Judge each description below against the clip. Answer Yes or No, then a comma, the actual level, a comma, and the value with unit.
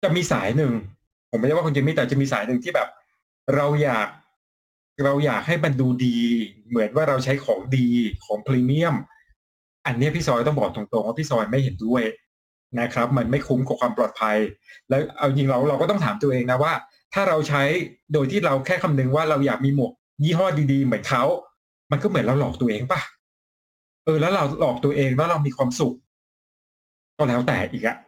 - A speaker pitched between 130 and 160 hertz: Yes, low, 135 Hz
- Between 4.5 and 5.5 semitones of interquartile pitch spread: No, average, 3.7 semitones